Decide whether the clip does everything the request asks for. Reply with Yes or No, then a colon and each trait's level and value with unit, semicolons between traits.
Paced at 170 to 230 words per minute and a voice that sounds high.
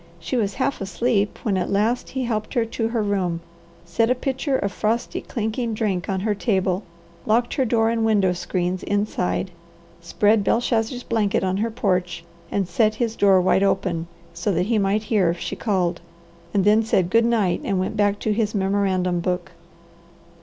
Yes: average, 180 wpm; high, 205 Hz